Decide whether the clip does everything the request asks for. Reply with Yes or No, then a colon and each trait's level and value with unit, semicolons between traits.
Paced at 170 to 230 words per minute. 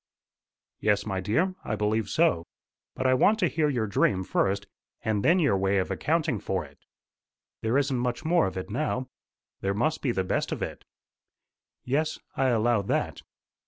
Yes: average, 175 wpm